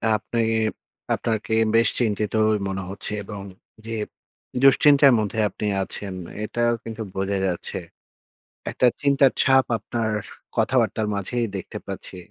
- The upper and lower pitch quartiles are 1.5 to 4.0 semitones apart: Yes, average, 2.9 semitones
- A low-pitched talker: Yes, low, 110 Hz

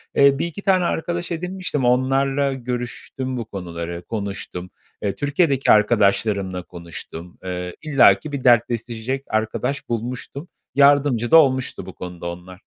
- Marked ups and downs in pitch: Yes, wide, 6.0 semitones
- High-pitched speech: No, low, 120 Hz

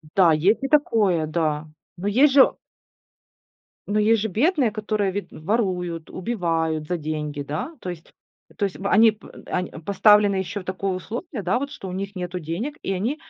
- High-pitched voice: Yes, high, 195 Hz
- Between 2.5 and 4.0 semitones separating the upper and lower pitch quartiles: No, average, 4.4 semitones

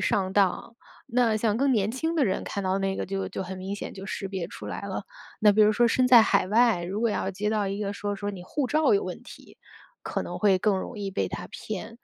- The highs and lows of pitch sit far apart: No, average, 3.1 semitones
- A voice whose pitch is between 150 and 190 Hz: No, high, 205 Hz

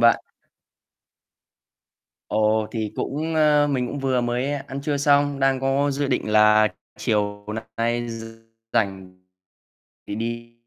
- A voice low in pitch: Yes, low, 120 Hz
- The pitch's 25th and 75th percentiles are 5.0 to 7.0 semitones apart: No, average, 4.5 semitones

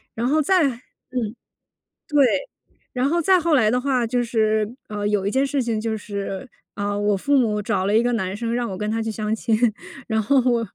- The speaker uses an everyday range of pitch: Yes, average, 3.5 semitones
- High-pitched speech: Yes, high, 230 Hz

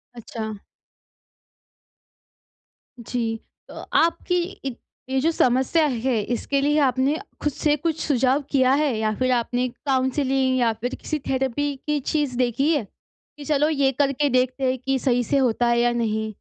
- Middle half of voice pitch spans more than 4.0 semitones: No, average, 2.9 semitones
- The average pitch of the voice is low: No, very high, 260 Hz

